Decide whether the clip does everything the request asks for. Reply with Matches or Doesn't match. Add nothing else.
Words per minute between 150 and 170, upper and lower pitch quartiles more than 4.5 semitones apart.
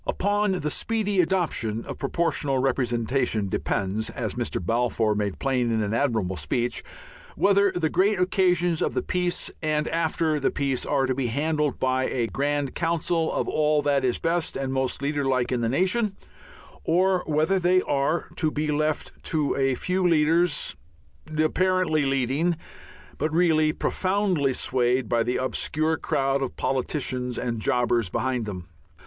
Matches